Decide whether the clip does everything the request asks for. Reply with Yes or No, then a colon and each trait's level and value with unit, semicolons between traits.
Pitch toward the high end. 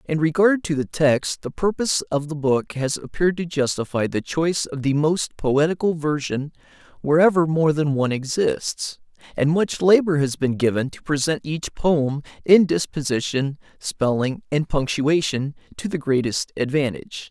No: medium, 150 Hz